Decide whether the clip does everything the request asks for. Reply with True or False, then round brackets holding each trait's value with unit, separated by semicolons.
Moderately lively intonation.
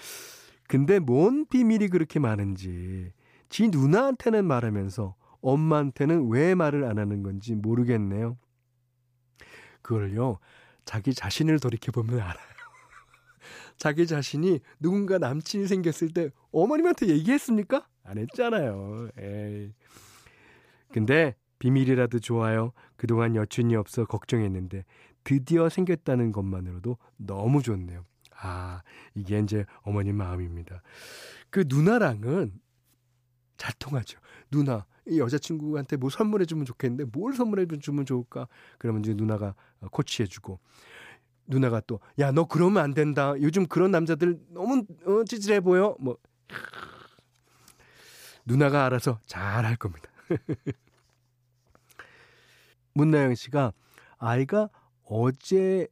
False (6.7 semitones)